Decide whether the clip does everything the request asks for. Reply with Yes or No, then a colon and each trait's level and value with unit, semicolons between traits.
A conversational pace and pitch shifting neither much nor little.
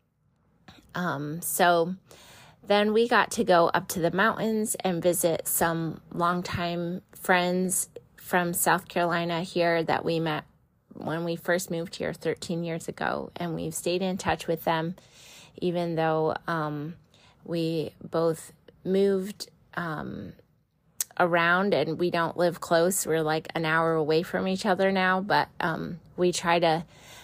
No: average, 145 wpm; narrow, 1.9 semitones